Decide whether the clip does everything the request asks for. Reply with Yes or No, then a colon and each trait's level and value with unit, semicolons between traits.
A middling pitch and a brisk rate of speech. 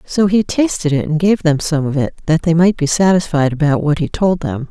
Yes: medium, 160 Hz; fast, 255 wpm